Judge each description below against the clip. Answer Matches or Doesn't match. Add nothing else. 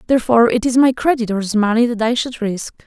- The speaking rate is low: Doesn't match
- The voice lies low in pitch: Doesn't match